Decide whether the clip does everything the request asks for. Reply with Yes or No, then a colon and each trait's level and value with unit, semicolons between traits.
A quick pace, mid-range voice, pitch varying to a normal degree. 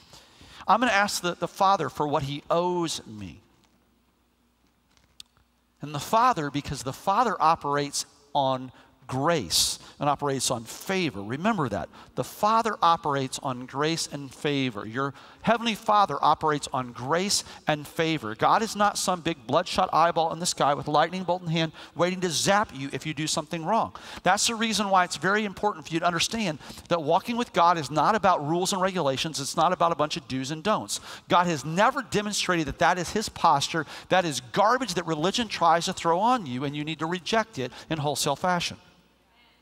No: average, 190 wpm; medium, 165 Hz; average, 4.6 semitones